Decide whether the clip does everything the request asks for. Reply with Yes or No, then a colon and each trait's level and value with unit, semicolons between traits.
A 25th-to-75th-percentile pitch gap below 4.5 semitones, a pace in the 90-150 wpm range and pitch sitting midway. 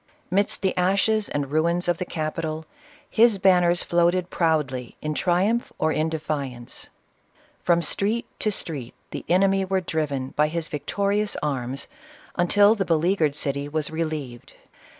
Yes: average, 4.1 semitones; average, 140 wpm; medium, 165 Hz